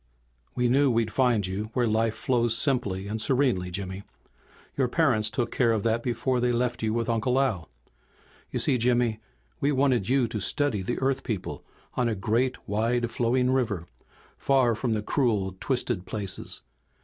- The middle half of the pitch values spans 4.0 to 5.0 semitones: No, average, 2.9 semitones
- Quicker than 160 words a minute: Yes, average, 170 wpm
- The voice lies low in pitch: Yes, low, 120 Hz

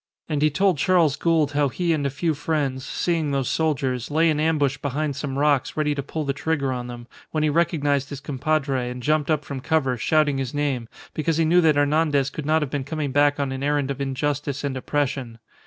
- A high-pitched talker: No, medium, 145 Hz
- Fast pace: Yes, fast, 220 wpm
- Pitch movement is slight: Yes, narrow, 2.3 semitones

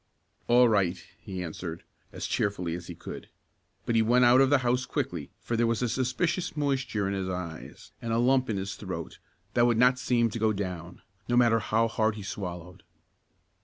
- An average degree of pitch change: Yes, average, 4.5 semitones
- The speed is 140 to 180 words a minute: No, average, 200 wpm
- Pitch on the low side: Yes, low, 115 Hz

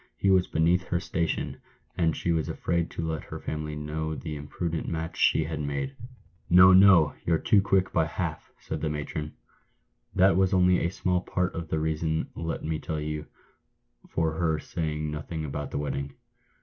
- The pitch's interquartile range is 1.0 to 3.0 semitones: Yes, average, 2.7 semitones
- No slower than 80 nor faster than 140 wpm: No, average, 190 wpm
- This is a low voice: Yes, very low, 80 Hz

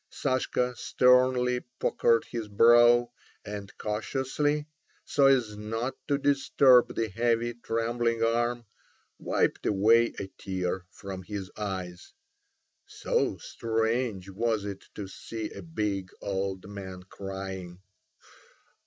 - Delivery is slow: Yes, slow, 100 wpm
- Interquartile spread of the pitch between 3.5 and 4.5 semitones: Yes, average, 3.8 semitones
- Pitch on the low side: Yes, low, 115 Hz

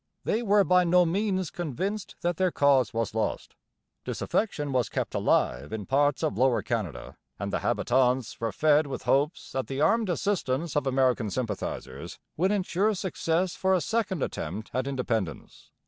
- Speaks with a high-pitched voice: No, medium, 145 Hz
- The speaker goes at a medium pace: Yes, average, 165 wpm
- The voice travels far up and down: Yes, wide, 6.9 semitones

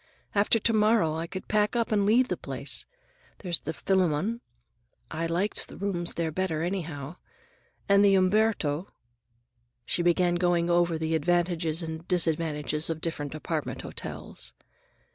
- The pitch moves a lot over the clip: No, average, 3.6 semitones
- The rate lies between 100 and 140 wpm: Yes, slow, 135 wpm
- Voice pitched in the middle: Yes, medium, 175 Hz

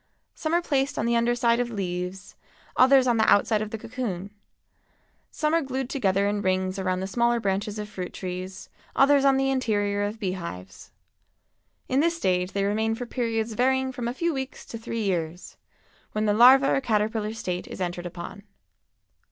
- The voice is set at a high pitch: Yes, high, 220 Hz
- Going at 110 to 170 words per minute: No, average, 185 wpm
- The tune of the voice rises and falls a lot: No, average, 5.0 semitones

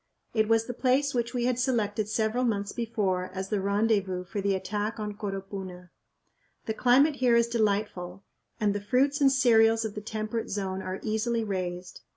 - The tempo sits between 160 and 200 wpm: Yes, average, 180 wpm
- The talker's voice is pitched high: Yes, high, 215 Hz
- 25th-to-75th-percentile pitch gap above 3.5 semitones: No, average, 3.1 semitones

